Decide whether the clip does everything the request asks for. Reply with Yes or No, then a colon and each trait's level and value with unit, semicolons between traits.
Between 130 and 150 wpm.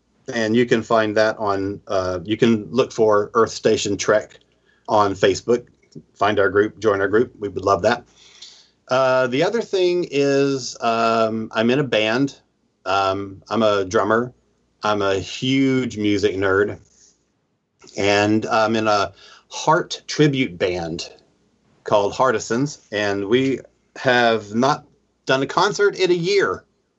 Yes: average, 140 wpm